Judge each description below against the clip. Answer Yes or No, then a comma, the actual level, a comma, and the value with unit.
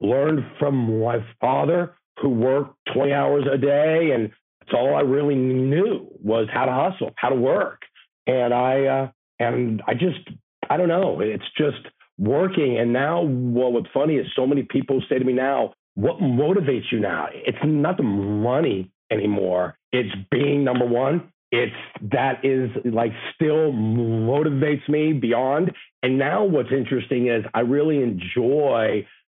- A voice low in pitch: Yes, low, 130 Hz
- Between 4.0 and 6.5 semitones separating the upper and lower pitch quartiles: No, average, 3.2 semitones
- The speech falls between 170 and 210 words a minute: No, average, 155 wpm